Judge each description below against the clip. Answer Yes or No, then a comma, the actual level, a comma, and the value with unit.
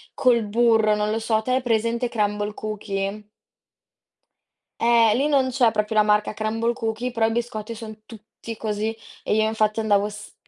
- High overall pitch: Yes, high, 220 Hz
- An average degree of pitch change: No, narrow, 1.7 semitones